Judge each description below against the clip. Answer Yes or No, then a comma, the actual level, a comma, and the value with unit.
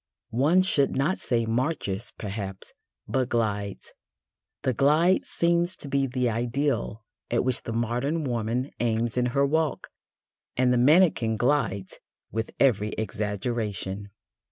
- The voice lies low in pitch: Yes, low, 120 Hz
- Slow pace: Yes, slow, 130 wpm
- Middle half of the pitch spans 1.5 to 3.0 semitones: No, average, 4.0 semitones